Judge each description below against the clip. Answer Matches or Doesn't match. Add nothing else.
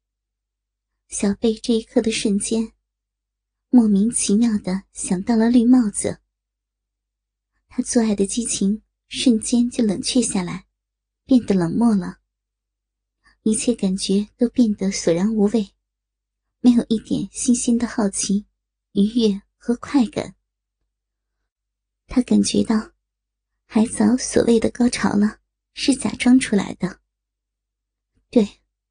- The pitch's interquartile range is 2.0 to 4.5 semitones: Matches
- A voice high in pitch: Matches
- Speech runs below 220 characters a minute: Matches